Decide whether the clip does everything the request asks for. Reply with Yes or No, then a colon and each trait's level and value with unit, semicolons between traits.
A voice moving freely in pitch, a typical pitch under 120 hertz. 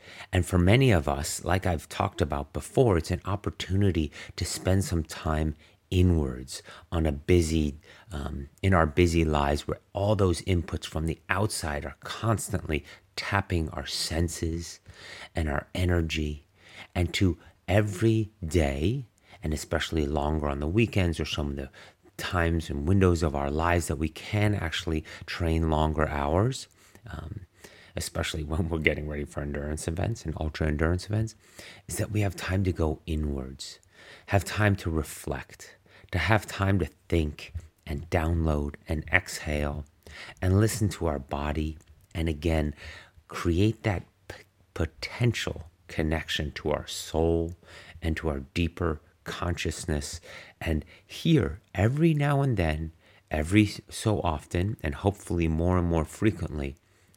No: average, 3.8 semitones; very low, 85 Hz